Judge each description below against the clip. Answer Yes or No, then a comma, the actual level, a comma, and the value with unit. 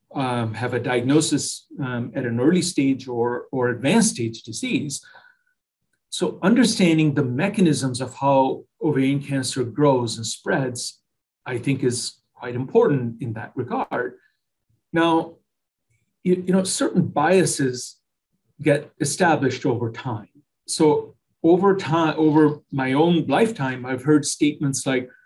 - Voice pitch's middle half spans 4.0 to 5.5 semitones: Yes, average, 4.7 semitones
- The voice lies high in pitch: No, medium, 140 Hz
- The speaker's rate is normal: No, slow, 130 wpm